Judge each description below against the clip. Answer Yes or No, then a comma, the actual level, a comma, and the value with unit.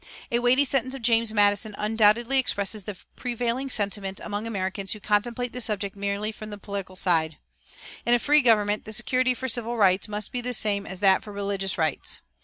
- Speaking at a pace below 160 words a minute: No, average, 195 wpm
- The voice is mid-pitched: No, high, 215 Hz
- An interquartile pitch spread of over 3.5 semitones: No, average, 3.1 semitones